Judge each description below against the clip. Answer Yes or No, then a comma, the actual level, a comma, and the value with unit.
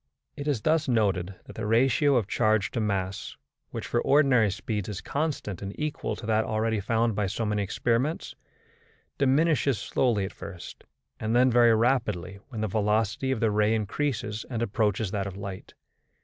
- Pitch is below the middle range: Yes, low, 110 Hz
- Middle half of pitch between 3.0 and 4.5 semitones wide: Yes, average, 3.4 semitones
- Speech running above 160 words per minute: Yes, average, 175 wpm